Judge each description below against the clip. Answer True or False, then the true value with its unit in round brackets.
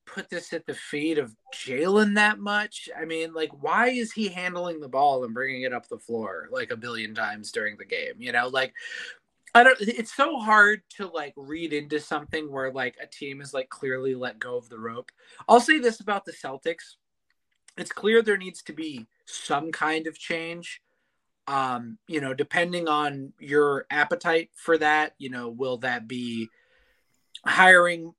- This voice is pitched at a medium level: True (165 Hz)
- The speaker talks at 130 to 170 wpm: False (185 wpm)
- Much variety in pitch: True (6.8 semitones)